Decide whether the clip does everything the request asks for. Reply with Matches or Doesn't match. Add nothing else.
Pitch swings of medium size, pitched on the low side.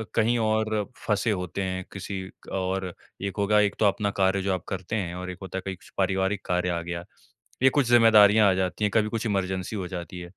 Doesn't match